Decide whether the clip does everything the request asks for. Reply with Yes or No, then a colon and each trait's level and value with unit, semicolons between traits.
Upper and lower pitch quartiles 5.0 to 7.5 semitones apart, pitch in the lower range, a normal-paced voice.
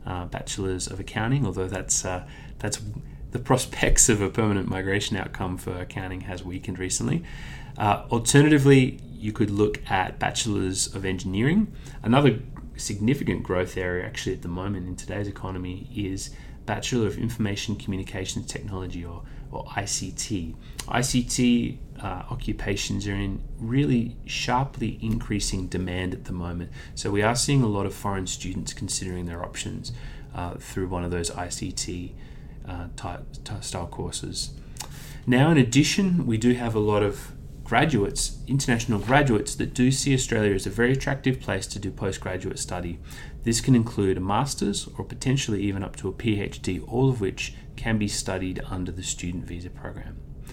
Yes: average, 5.3 semitones; low, 110 Hz; average, 155 wpm